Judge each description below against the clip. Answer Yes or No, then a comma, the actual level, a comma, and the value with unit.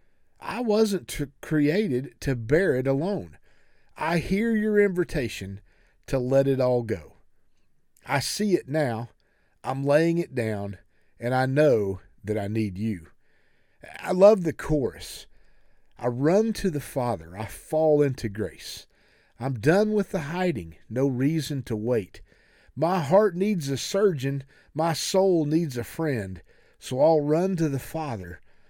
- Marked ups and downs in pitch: Yes, wide, 6.6 semitones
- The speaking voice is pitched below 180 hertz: Yes, medium, 140 Hz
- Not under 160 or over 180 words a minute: No, average, 145 wpm